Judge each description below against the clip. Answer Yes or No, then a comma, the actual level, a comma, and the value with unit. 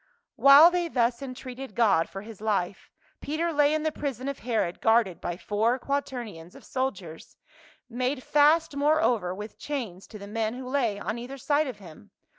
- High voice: Yes, high, 245 Hz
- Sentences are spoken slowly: No, average, 175 wpm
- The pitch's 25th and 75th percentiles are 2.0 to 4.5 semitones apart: No, average, 5.3 semitones